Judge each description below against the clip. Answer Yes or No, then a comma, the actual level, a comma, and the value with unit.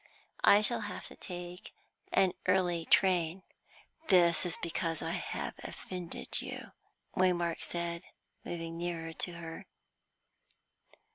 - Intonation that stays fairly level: Yes, narrow, 1.6 semitones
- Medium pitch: Yes, medium, 175 Hz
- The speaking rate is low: Yes, slow, 115 wpm